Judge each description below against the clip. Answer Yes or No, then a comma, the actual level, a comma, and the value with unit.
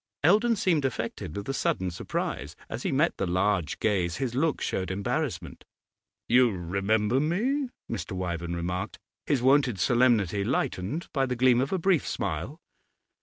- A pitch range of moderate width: No, wide, 6.9 semitones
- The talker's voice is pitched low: Yes, low, 120 Hz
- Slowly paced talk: No, average, 155 wpm